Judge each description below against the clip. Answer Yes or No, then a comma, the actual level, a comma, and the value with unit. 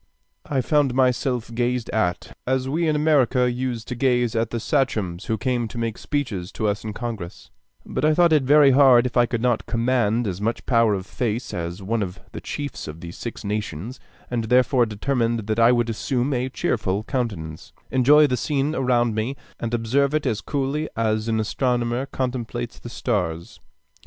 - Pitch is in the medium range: No, low, 120 Hz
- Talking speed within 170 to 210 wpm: Yes, average, 185 wpm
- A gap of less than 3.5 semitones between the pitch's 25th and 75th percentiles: Yes, average, 3.1 semitones